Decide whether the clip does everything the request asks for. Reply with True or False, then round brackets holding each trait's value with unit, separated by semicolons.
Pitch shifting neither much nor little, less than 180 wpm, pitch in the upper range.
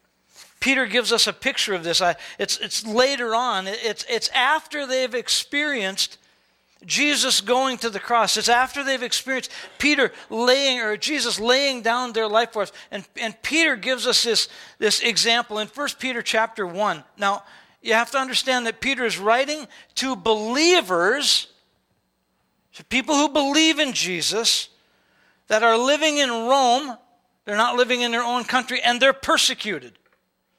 True (3.2 semitones; 155 wpm; 240 Hz)